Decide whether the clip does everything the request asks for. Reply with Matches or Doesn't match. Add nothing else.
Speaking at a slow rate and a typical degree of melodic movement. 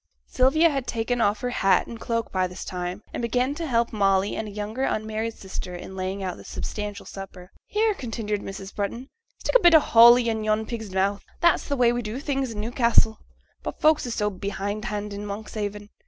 Doesn't match